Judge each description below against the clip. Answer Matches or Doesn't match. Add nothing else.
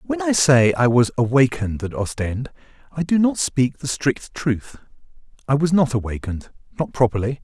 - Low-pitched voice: Matches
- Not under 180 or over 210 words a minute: Doesn't match